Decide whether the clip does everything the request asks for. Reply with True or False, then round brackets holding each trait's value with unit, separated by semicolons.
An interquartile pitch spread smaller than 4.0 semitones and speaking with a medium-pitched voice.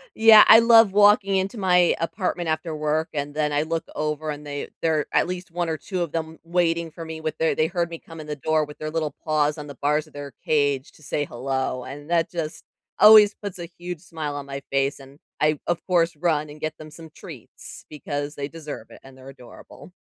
True (2.7 semitones; 155 Hz)